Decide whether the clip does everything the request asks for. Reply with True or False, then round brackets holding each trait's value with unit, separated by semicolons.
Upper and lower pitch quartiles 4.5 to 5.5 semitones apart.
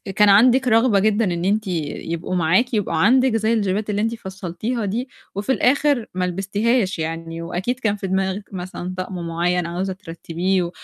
False (4.0 semitones)